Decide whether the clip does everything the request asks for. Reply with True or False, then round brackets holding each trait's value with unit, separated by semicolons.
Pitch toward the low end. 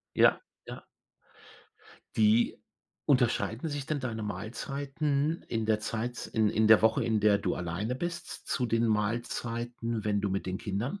True (115 Hz)